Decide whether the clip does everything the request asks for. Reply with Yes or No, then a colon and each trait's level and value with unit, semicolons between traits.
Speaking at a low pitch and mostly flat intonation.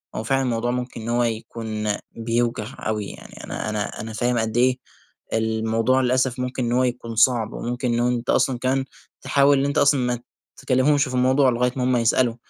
Yes: low, 120 Hz; narrow, 2.1 semitones